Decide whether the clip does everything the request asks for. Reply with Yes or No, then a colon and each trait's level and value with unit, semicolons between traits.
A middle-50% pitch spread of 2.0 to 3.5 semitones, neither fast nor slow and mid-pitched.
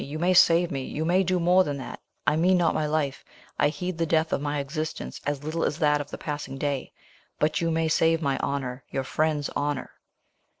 No: narrow, 2.6 semitones; fast, 220 wpm; medium, 155 Hz